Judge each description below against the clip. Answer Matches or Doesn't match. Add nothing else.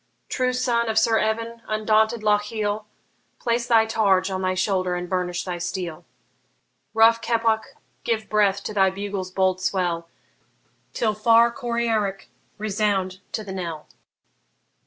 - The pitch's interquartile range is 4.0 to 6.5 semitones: Doesn't match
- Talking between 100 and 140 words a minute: Matches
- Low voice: Doesn't match